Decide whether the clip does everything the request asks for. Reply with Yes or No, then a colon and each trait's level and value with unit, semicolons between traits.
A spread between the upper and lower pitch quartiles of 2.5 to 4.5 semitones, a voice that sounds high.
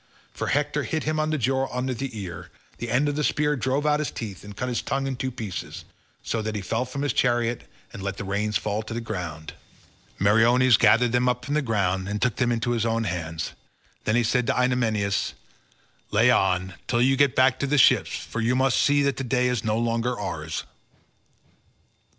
No: average, 3.7 semitones; low, 120 Hz